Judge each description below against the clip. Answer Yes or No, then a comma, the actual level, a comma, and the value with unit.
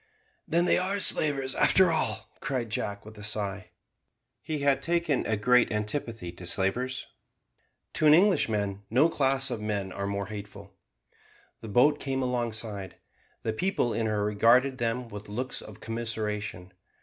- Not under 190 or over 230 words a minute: No, average, 150 wpm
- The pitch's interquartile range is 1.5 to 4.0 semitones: No, average, 4.8 semitones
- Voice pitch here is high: No, low, 115 Hz